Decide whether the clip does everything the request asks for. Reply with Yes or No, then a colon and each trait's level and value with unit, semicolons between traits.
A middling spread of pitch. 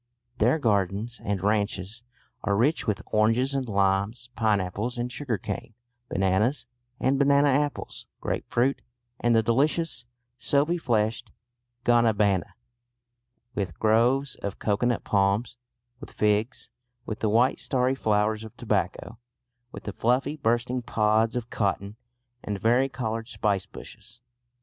Yes: average, 3.2 semitones